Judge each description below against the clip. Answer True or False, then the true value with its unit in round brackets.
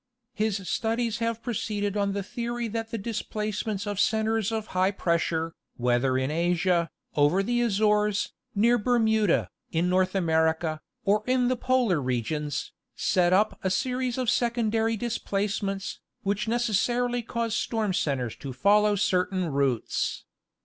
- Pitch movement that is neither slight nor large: True (4.4 semitones)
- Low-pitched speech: False (205 Hz)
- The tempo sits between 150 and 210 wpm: False (140 wpm)